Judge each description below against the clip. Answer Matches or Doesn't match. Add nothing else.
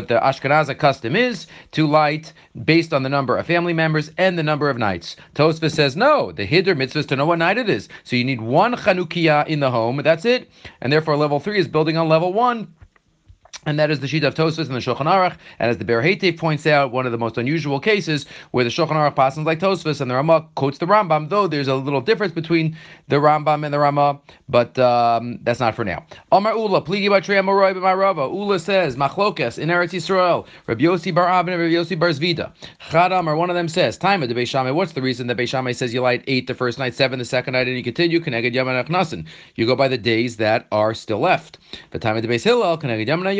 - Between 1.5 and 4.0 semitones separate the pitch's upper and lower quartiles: Doesn't match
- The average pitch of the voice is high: Doesn't match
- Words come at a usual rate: Doesn't match